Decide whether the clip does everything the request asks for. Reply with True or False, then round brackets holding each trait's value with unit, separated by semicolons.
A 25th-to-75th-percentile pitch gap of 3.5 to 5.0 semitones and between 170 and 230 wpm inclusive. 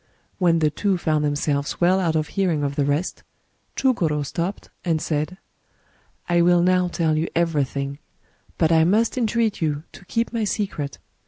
True (3.8 semitones; 175 wpm)